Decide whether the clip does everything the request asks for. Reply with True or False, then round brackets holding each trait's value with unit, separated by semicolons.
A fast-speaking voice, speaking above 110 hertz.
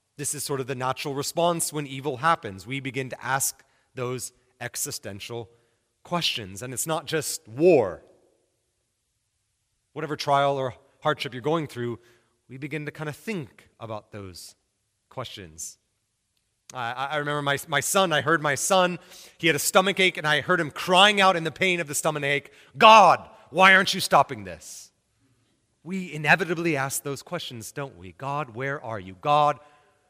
False (165 wpm; 140 Hz)